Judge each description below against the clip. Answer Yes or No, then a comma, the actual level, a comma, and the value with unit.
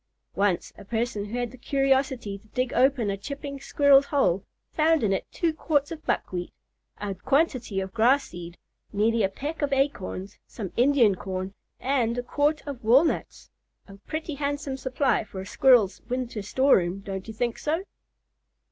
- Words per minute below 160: No, average, 165 wpm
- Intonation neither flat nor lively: No, wide, 5.9 semitones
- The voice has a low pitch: No, high, 245 Hz